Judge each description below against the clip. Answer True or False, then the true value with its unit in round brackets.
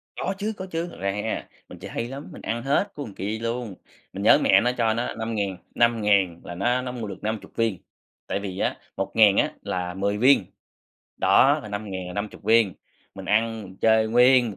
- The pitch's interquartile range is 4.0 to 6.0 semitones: False (3.4 semitones)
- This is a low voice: True (110 Hz)